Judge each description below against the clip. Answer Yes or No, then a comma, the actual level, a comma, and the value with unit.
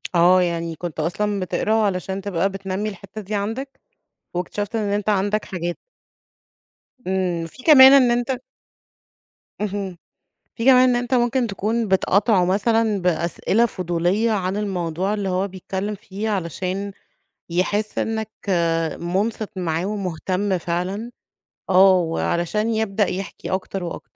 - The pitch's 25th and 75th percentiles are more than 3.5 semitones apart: No, average, 3.0 semitones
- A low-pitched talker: No, high, 195 Hz